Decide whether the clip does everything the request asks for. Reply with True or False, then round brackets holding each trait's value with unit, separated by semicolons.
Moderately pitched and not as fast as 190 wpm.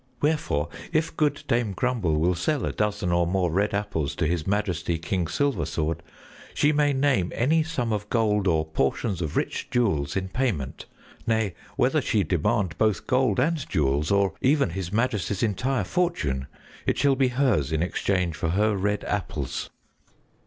False (100 Hz; 165 wpm)